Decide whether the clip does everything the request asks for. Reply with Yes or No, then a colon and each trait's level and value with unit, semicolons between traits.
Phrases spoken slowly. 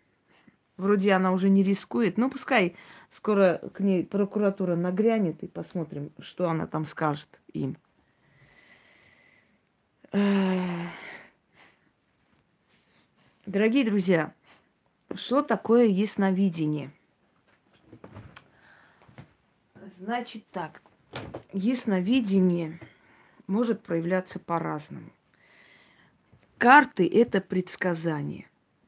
Yes: slow, 70 wpm